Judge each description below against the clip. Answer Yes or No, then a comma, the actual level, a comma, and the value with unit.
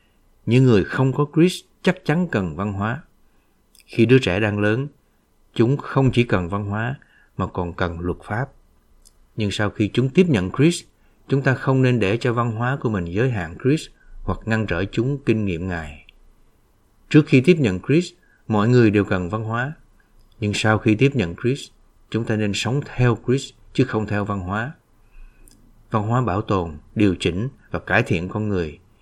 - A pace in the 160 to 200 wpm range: Yes, average, 190 wpm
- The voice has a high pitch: No, low, 110 Hz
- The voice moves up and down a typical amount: Yes, average, 4.5 semitones